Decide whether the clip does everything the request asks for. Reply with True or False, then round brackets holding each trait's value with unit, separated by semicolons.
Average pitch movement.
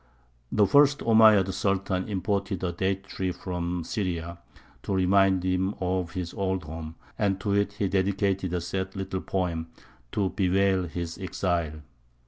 False (1.8 semitones)